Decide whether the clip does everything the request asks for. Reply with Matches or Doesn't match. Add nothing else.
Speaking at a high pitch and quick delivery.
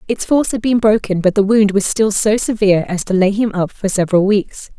Matches